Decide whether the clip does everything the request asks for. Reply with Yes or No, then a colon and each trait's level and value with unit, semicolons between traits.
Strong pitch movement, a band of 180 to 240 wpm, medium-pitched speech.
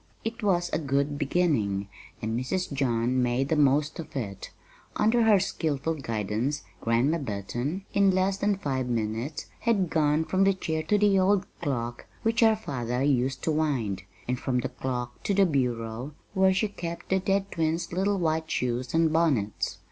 No: wide, 7.2 semitones; average, 170 wpm; medium, 150 Hz